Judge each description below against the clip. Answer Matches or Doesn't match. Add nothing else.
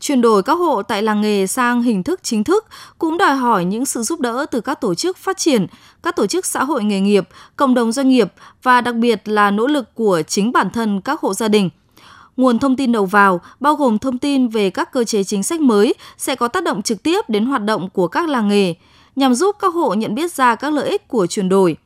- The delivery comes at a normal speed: Doesn't match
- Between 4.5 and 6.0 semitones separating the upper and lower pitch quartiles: Matches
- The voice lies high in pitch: Matches